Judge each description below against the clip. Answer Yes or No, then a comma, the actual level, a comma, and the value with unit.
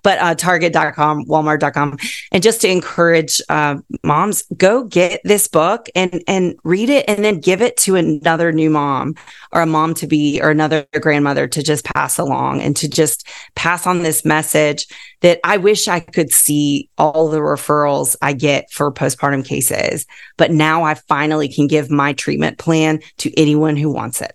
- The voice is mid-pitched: Yes, medium, 155 Hz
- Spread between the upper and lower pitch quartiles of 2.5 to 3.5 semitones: Yes, average, 3.0 semitones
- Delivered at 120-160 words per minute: No, average, 180 wpm